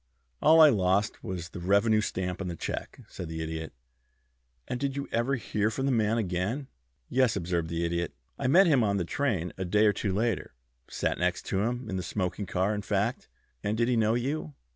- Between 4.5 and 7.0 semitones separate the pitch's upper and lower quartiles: Yes, average, 5.0 semitones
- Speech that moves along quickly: Yes, fast, 210 wpm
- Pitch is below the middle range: Yes, low, 105 Hz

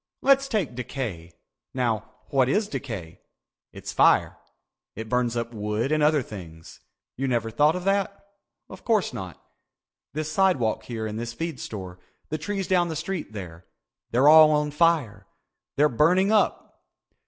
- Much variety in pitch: Yes, wide, 7.2 semitones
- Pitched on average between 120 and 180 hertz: Yes, low, 135 Hz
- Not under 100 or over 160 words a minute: Yes, average, 150 wpm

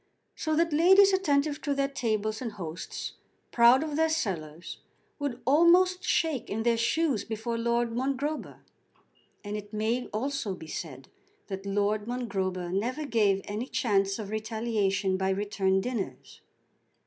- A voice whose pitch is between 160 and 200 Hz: No, high, 230 Hz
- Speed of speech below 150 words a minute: Yes, average, 140 wpm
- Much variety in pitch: Yes, wide, 5.9 semitones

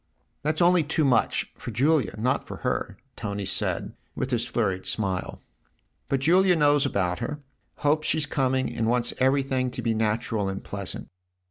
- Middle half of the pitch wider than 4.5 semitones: Yes, average, 5.2 semitones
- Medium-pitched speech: No, low, 130 Hz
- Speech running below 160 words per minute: No, average, 165 wpm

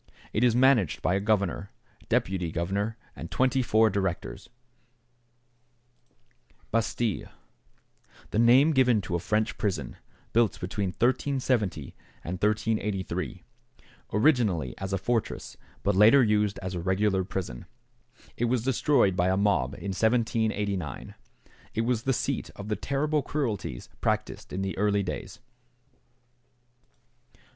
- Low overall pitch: Yes, low, 105 Hz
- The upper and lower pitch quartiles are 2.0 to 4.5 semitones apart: Yes, average, 3.7 semitones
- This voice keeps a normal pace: No, slow, 125 wpm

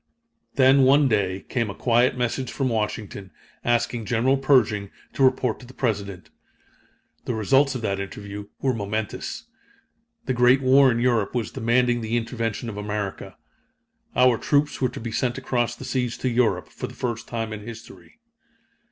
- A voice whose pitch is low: Yes, low, 120 Hz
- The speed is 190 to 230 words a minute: No, average, 165 wpm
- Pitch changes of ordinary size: Yes, average, 3.1 semitones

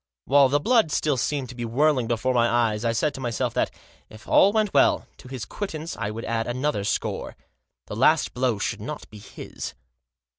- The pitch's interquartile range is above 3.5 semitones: Yes, average, 4.5 semitones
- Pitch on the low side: Yes, low, 125 Hz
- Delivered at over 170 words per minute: Yes, average, 200 wpm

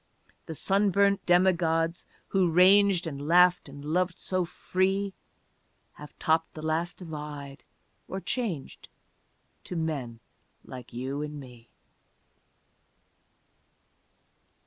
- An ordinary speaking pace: No, slow, 100 wpm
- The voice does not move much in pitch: No, average, 3.9 semitones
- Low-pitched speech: No, medium, 165 Hz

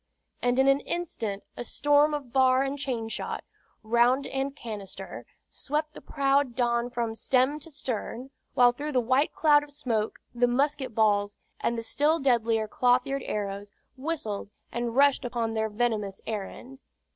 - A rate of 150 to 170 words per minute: Yes, average, 155 wpm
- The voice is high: Yes, very high, 250 Hz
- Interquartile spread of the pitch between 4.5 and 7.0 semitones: No, average, 3.7 semitones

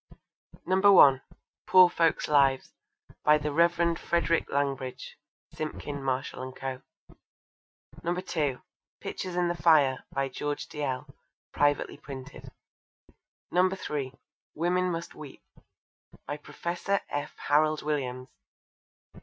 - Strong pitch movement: No, average, 3.9 semitones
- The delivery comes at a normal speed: No, slow, 100 wpm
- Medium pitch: Yes, medium, 150 Hz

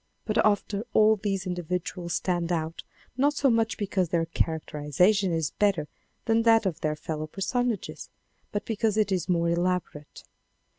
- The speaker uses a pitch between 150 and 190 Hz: Yes, medium, 185 Hz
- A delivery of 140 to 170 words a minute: Yes, average, 155 wpm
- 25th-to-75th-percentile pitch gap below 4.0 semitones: No, average, 4.3 semitones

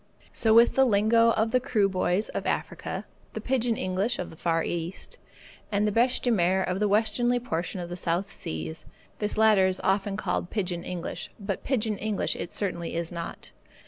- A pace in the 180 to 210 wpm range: Yes, average, 190 wpm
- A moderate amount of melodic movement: Yes, average, 4.0 semitones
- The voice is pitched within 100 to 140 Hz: No, high, 200 Hz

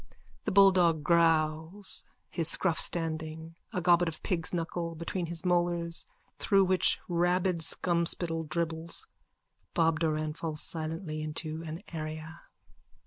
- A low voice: No, medium, 165 Hz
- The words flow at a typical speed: No, slow, 120 wpm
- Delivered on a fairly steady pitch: Yes, narrow, 1.7 semitones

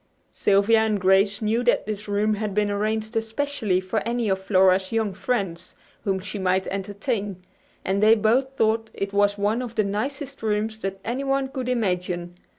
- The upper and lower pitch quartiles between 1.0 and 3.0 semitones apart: Yes, narrow, 2.5 semitones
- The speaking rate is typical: Yes, average, 170 wpm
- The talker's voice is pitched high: Yes, high, 210 Hz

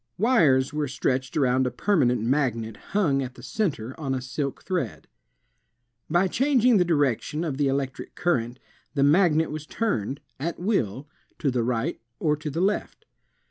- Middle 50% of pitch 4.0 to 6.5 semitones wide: Yes, average, 5.1 semitones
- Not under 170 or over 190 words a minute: No, average, 160 wpm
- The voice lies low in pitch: No, medium, 145 Hz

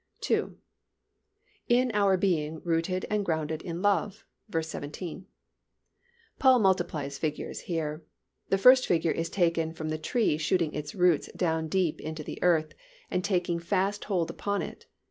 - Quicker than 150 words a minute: No, average, 145 wpm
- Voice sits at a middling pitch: Yes, medium, 170 Hz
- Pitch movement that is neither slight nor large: Yes, average, 3.5 semitones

